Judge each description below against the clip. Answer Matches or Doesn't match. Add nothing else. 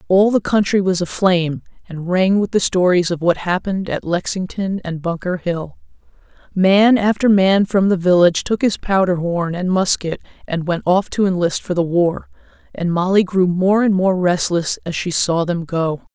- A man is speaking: Doesn't match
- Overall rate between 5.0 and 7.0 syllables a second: Doesn't match